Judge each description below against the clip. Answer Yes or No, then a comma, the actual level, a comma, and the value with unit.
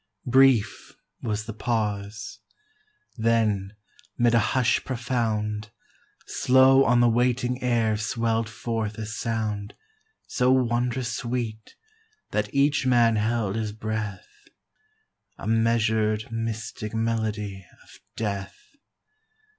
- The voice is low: Yes, low, 115 Hz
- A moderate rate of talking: No, slow, 100 wpm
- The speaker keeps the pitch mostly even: Yes, narrow, 2.0 semitones